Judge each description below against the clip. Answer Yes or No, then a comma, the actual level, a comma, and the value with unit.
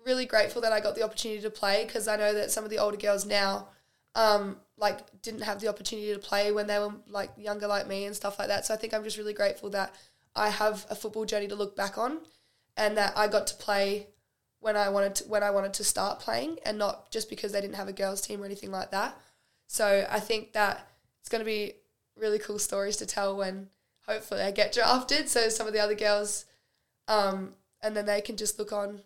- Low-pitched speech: No, high, 210 Hz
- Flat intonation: Yes, narrow, 1.1 semitones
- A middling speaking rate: No, fast, 240 wpm